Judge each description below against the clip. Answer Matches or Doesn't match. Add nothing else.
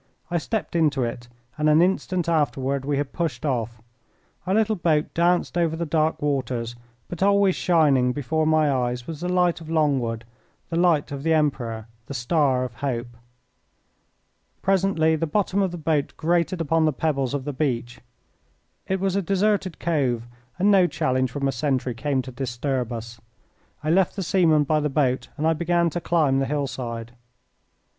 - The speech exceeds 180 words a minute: Doesn't match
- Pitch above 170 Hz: Doesn't match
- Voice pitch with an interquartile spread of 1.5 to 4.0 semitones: Doesn't match